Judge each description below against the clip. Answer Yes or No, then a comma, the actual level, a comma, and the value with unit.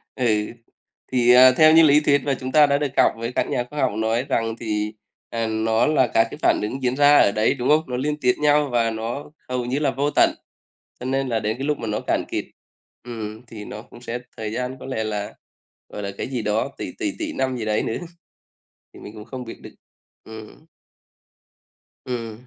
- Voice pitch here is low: Yes, low, 125 Hz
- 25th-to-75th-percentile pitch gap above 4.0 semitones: No, average, 3.7 semitones